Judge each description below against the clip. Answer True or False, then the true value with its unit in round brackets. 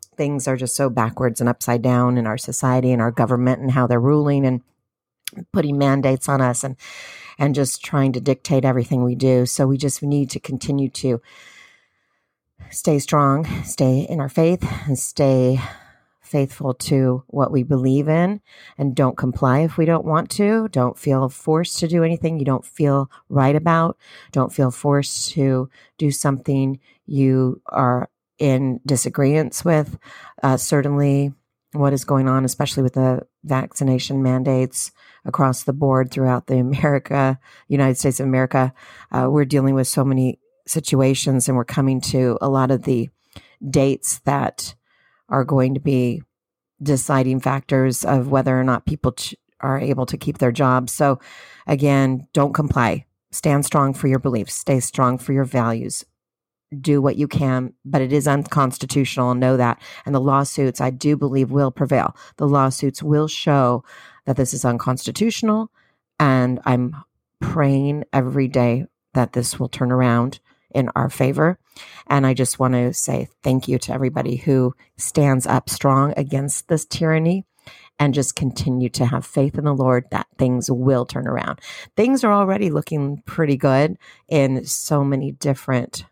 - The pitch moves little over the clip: True (2.0 semitones)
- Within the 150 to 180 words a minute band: True (160 wpm)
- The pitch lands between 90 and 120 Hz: False (135 Hz)